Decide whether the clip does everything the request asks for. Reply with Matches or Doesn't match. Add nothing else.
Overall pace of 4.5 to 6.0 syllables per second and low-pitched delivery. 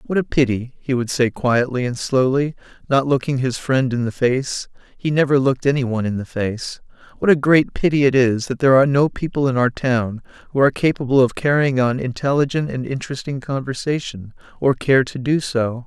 Matches